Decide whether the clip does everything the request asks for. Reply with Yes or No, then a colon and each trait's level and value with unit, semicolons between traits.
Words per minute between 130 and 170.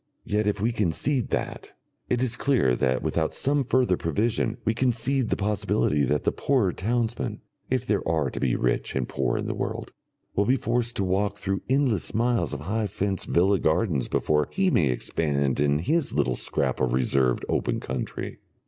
No: average, 185 wpm